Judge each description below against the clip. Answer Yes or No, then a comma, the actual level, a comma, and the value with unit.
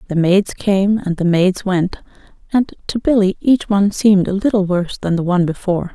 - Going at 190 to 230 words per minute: Yes, average, 200 wpm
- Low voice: No, high, 190 Hz